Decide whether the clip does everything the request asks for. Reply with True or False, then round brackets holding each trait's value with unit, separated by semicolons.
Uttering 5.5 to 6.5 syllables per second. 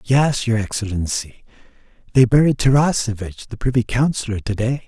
False (5.2 syllables/s)